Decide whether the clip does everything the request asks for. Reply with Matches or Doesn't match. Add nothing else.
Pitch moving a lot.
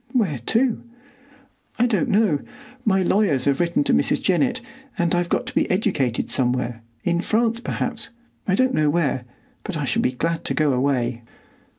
Matches